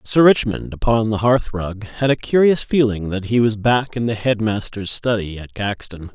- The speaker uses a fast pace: No, average, 195 wpm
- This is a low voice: Yes, low, 110 Hz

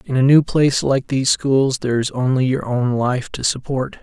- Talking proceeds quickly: Yes, fast, 225 wpm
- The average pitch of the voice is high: No, low, 130 Hz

